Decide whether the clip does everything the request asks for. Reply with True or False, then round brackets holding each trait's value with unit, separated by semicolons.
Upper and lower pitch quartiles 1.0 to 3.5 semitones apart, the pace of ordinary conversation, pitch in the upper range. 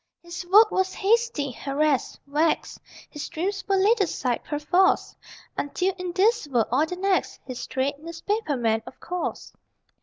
False (5.1 semitones; 150 wpm; 345 Hz)